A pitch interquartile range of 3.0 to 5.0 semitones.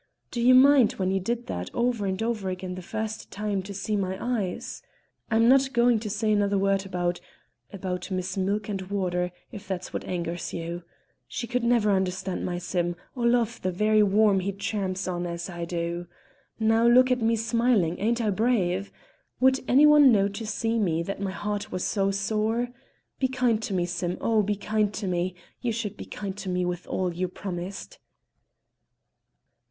Yes: average, 3.7 semitones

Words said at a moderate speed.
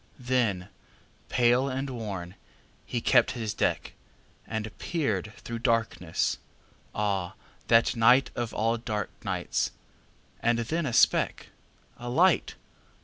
No: slow, 100 wpm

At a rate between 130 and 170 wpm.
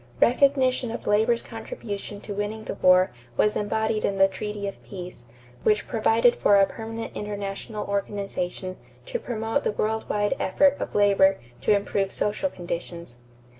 Yes: average, 150 wpm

